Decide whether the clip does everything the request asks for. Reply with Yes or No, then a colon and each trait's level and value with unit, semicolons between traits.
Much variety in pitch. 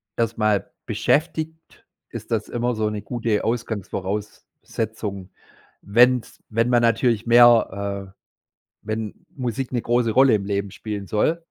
No: narrow, 2.6 semitones